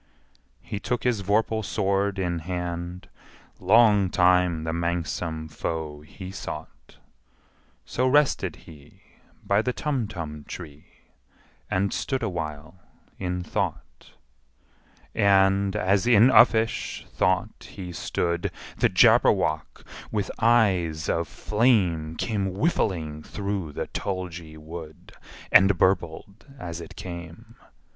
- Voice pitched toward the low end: Yes, very low, 90 Hz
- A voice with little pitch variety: No, average, 3.7 semitones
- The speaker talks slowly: Yes, slow, 105 wpm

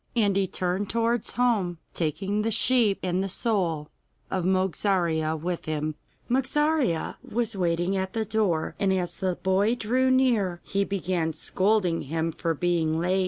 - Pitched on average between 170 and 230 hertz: Yes, high, 190 Hz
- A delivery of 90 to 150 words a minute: No, average, 160 wpm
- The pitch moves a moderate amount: Yes, average, 4.3 semitones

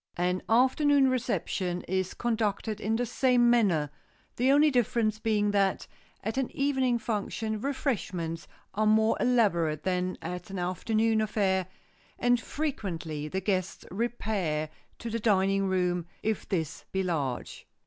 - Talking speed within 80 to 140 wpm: Yes, slow, 135 wpm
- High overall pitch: Yes, high, 210 Hz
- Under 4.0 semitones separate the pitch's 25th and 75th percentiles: No, average, 4.6 semitones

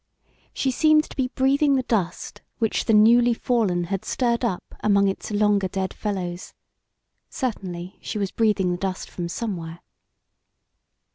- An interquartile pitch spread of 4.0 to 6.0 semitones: Yes, average, 4.6 semitones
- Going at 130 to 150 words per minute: Yes, average, 145 wpm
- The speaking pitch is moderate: No, high, 210 Hz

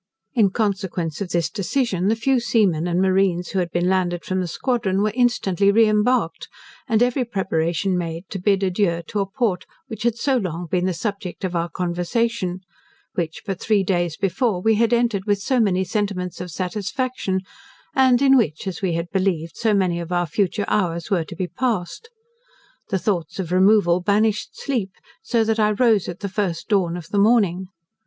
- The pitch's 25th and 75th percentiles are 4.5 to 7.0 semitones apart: No, average, 3.8 semitones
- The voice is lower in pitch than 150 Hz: No, high, 195 Hz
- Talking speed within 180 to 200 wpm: Yes, average, 190 wpm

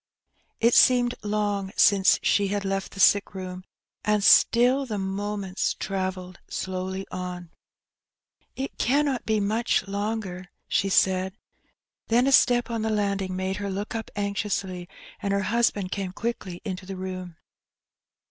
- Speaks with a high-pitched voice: Yes, high, 200 Hz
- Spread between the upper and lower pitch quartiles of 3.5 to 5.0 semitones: No, narrow, 2.5 semitones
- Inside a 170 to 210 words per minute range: No, average, 140 wpm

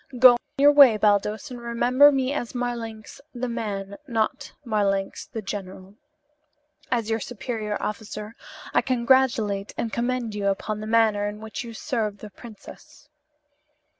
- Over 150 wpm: No, average, 140 wpm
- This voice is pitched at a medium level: No, high, 225 Hz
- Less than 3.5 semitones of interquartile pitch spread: Yes, average, 2.8 semitones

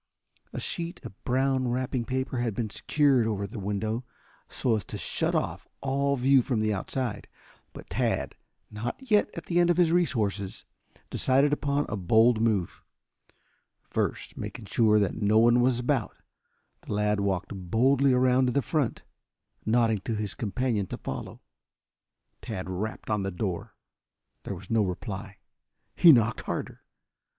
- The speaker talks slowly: No, average, 155 wpm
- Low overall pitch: Yes, low, 115 Hz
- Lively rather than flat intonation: No, average, 4.1 semitones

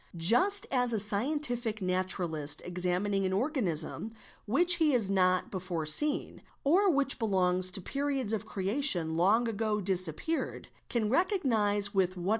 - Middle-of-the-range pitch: No, high, 205 Hz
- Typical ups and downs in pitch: No, wide, 6.3 semitones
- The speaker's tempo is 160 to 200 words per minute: No, slow, 135 wpm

